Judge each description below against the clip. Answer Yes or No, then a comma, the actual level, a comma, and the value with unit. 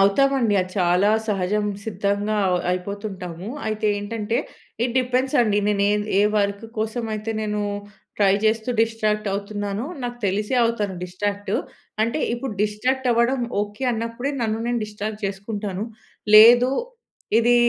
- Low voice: No, high, 210 Hz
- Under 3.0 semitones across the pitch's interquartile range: Yes, narrow, 2.4 semitones